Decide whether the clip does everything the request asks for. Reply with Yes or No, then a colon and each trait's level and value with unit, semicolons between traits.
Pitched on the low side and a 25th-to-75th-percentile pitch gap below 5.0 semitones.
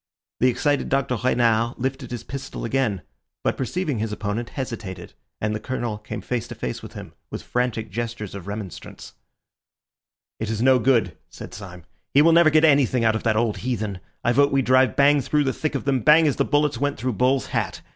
Yes: low, 125 Hz; average, 4.0 semitones